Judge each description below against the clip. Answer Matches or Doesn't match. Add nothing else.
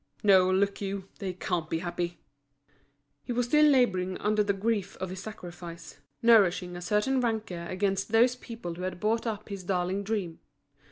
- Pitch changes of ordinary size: Matches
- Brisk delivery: Doesn't match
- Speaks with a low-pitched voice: Doesn't match